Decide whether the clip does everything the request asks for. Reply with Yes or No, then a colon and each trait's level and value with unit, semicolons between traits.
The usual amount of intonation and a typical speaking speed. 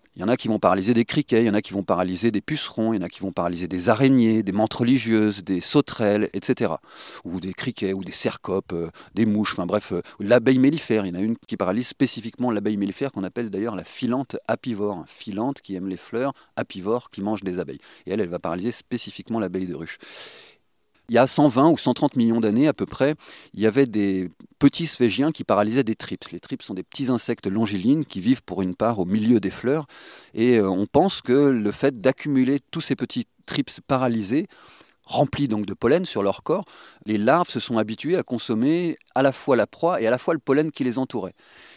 No: average, 5.0 semitones; fast, 225 wpm